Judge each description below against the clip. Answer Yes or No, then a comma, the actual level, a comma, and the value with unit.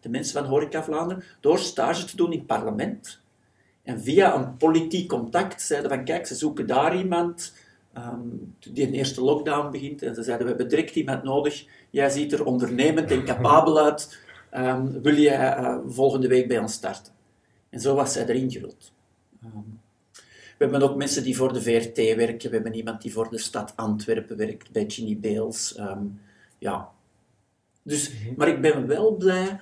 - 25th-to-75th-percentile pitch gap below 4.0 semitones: No, average, 4.9 semitones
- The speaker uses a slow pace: No, average, 185 wpm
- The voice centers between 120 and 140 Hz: Yes, low, 135 Hz